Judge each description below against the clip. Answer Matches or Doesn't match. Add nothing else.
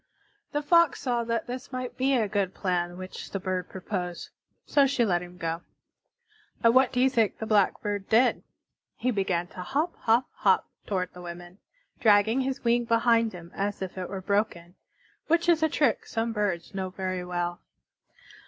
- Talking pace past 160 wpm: Matches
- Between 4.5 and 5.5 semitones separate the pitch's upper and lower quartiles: Matches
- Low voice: Doesn't match